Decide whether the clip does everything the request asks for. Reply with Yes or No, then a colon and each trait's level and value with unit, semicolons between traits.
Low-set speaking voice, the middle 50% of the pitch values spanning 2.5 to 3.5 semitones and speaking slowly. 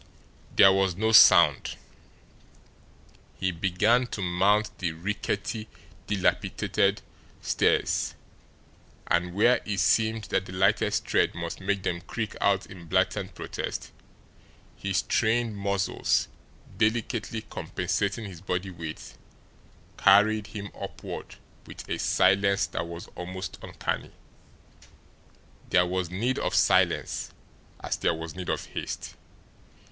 Yes: very low, 95 Hz; average, 2.9 semitones; slow, 115 wpm